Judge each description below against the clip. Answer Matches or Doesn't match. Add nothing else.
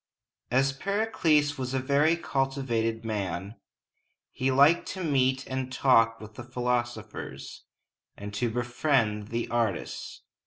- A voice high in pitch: Doesn't match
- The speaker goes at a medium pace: Doesn't match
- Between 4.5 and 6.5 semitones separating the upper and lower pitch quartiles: Doesn't match